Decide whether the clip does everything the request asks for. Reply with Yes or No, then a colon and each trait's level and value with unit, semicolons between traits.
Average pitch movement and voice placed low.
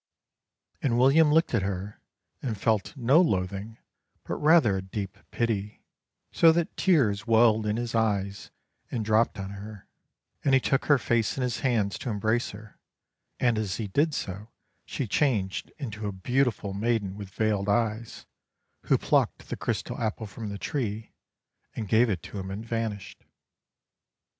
Yes: average, 3.1 semitones; low, 110 Hz